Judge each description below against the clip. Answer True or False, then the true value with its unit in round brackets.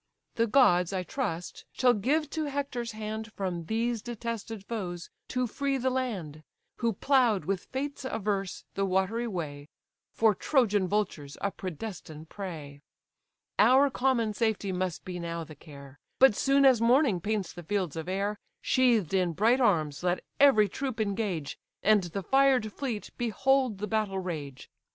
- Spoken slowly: False (155 wpm)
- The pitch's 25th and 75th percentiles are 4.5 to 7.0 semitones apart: True (5.2 semitones)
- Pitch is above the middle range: True (210 Hz)